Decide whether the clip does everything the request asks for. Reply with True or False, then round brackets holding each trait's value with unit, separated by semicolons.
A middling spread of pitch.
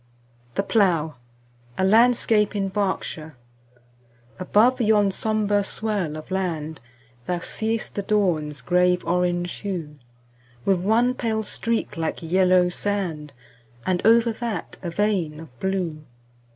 True (4.1 semitones)